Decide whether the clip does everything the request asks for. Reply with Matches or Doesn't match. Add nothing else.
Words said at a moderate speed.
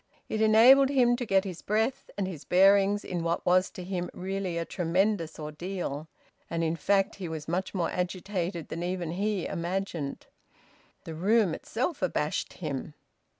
Matches